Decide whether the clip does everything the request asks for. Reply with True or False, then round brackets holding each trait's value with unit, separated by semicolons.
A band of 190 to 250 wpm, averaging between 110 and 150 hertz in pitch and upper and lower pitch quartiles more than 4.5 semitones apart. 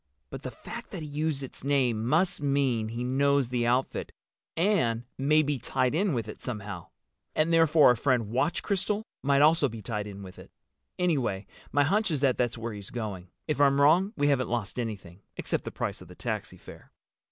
True (200 wpm; 135 Hz; 4.9 semitones)